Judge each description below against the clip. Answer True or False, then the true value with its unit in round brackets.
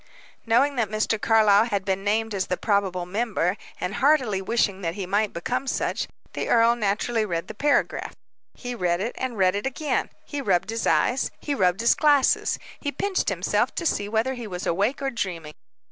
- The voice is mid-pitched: False (215 Hz)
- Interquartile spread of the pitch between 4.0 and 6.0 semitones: True (4.3 semitones)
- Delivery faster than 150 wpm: True (190 wpm)